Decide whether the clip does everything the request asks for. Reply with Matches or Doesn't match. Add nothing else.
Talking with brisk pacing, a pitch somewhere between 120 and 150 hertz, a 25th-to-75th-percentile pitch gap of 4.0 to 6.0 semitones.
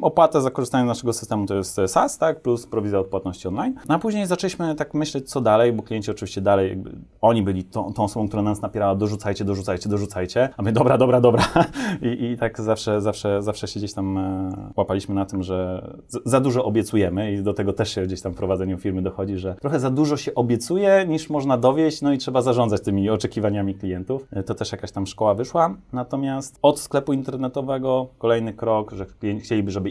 Doesn't match